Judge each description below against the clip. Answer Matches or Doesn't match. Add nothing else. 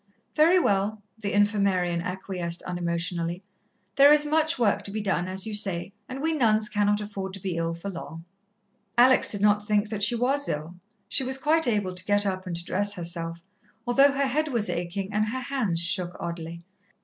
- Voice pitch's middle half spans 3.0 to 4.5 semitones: Doesn't match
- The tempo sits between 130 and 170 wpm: Doesn't match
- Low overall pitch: Doesn't match